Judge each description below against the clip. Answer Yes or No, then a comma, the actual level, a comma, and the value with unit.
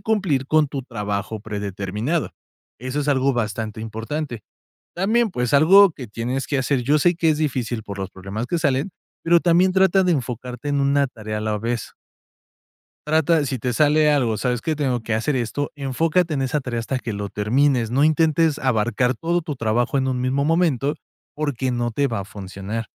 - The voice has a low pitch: Yes, low, 130 Hz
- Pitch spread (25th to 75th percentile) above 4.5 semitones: Yes, average, 5.0 semitones